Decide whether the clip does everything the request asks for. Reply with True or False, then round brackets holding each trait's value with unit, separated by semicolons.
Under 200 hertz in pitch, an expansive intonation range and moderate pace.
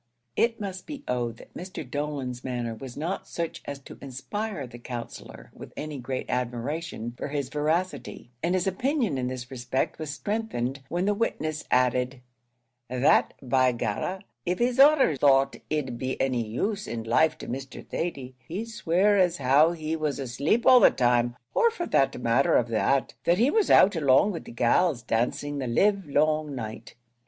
True (140 Hz; 6.4 semitones; 175 wpm)